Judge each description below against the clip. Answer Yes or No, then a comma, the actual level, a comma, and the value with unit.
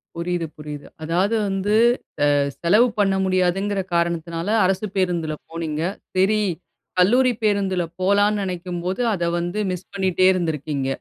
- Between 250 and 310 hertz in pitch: No, medium, 185 Hz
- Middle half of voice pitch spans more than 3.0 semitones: No, average, 2.7 semitones